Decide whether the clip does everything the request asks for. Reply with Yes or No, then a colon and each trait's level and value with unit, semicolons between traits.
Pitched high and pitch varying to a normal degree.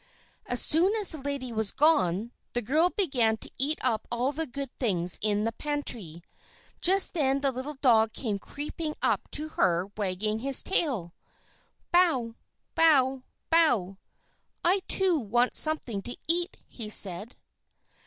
No: very high, 255 Hz; wide, 6.2 semitones